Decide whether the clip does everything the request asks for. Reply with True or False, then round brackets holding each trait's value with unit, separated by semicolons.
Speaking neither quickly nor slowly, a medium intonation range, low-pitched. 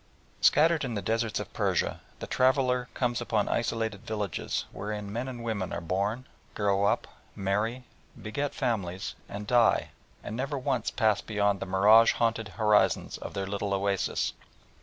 True (155 wpm; 3.1 semitones; 110 Hz)